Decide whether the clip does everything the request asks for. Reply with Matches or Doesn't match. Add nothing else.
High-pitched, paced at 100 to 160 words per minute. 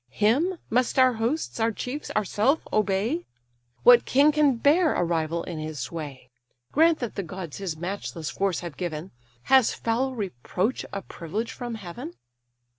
Matches